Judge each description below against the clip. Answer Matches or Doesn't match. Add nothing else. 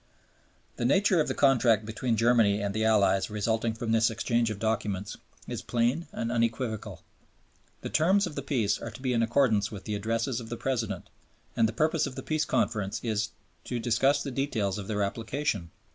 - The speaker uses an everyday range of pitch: Matches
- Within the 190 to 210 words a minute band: Matches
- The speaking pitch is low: Matches